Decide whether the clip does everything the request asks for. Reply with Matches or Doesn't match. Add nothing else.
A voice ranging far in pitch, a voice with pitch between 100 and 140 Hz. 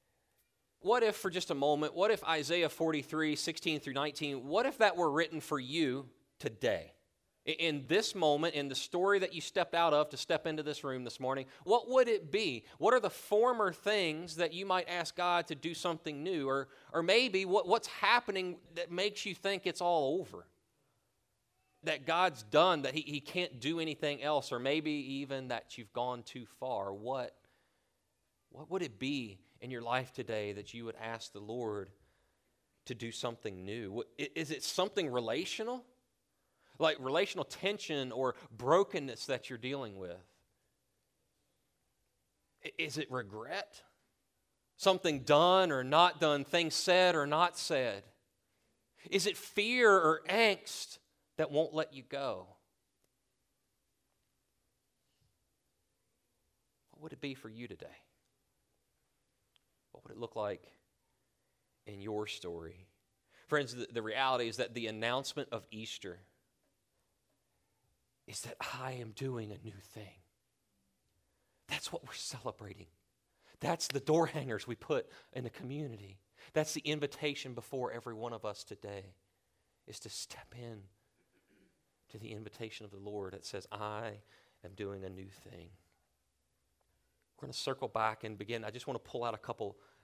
Matches